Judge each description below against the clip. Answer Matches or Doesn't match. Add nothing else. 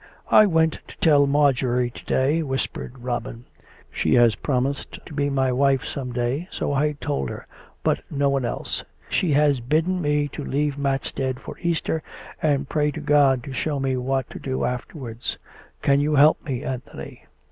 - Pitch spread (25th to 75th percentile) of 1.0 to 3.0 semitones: Matches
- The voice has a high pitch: Doesn't match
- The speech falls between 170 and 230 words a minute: Matches